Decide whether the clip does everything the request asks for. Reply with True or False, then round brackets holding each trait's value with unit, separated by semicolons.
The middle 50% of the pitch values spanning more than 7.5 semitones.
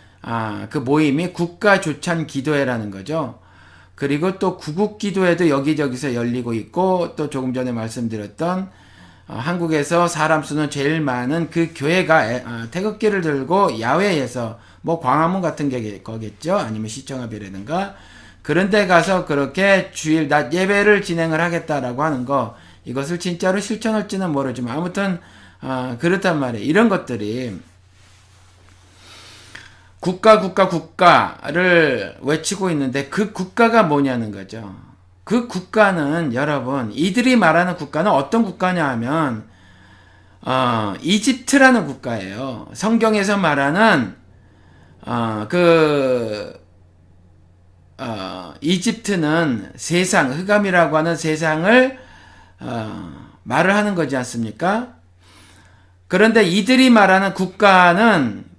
True (8.7 semitones)